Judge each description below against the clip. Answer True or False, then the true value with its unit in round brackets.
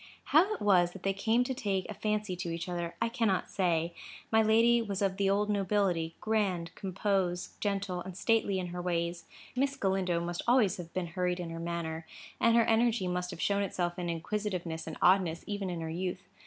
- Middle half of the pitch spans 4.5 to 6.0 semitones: False (3.2 semitones)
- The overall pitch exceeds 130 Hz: True (190 Hz)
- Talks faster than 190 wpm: True (200 wpm)